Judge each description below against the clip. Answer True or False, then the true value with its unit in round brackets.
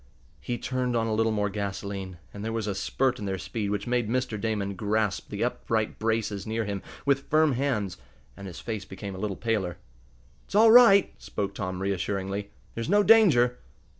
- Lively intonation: False (3.7 semitones)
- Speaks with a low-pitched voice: True (110 Hz)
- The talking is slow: False (190 wpm)